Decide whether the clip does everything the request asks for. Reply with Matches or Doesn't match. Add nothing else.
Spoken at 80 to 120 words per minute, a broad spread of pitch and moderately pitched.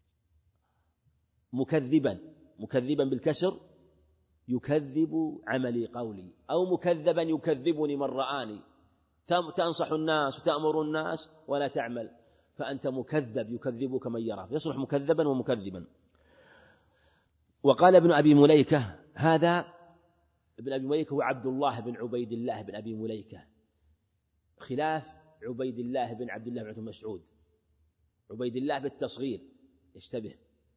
Doesn't match